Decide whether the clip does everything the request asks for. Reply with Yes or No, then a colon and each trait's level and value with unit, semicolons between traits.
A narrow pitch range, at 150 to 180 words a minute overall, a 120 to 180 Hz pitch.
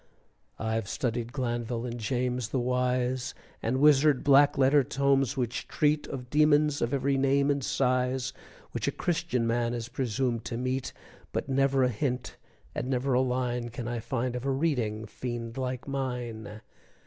Yes: narrow, 2.2 semitones; average, 160 wpm; low, 125 Hz